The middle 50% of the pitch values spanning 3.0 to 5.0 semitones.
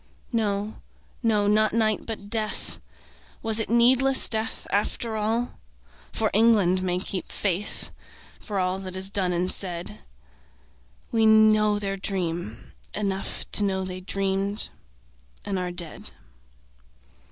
No: narrow, 2.6 semitones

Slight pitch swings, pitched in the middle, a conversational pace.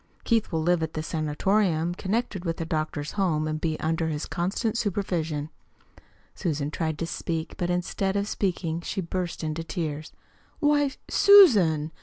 No: average, 3.6 semitones; medium, 170 Hz; average, 155 wpm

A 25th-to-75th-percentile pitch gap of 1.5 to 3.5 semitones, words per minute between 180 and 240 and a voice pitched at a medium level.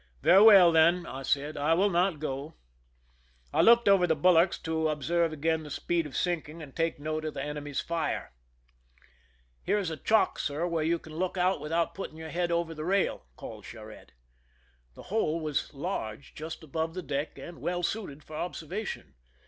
Yes: average, 2.8 semitones; average, 190 wpm; medium, 160 Hz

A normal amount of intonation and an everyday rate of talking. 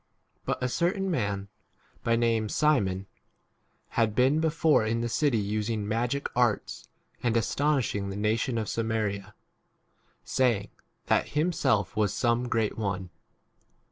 No: average, 3.7 semitones; slow, 130 wpm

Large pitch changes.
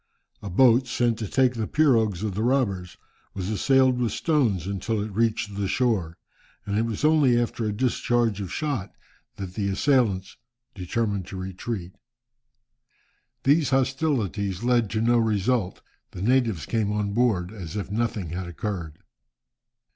No: average, 4.0 semitones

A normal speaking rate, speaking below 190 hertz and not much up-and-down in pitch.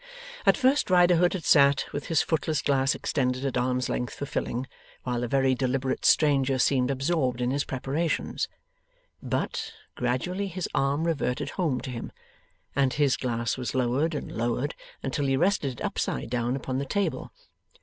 No: average, 165 wpm; low, 135 Hz; average, 3.3 semitones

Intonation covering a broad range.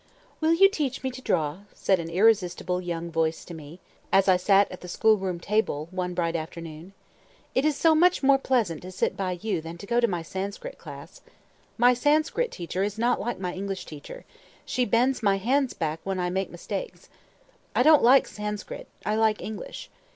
Yes: wide, 5.8 semitones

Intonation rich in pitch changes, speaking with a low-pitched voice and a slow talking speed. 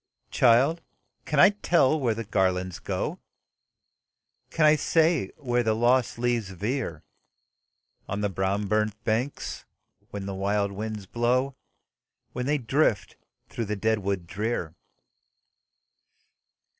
No: average, 4.7 semitones; low, 110 Hz; slow, 120 wpm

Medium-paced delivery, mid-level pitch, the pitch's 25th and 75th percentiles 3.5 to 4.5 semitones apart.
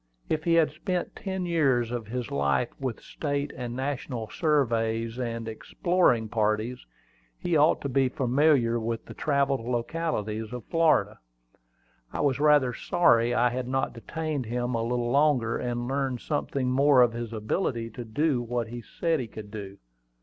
No: average, 165 wpm; low, 125 Hz; average, 3.9 semitones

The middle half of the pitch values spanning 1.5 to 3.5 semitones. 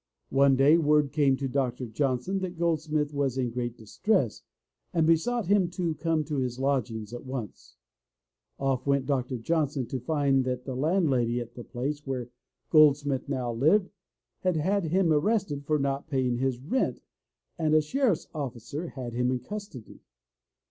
No: average, 4.0 semitones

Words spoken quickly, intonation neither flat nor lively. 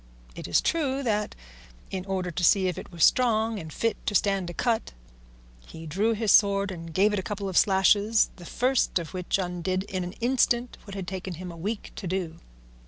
Yes: fast, 210 wpm; average, 3.3 semitones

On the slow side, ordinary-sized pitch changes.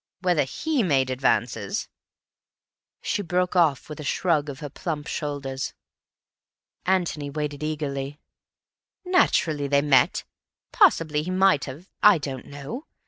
Yes: slow, 120 wpm; average, 4.1 semitones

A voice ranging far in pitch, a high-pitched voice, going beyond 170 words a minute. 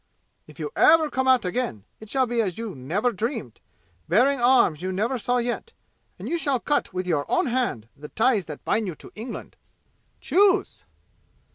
Yes: wide, 6.1 semitones; high, 230 Hz; average, 180 wpm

